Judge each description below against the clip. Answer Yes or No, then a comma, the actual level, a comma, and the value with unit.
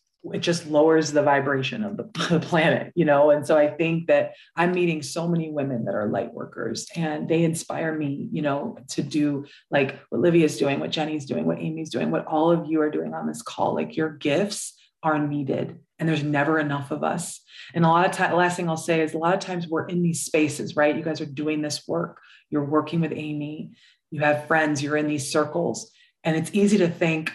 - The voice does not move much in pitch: Yes, narrow, 2.0 semitones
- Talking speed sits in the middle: No, fast, 230 wpm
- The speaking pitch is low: No, medium, 155 Hz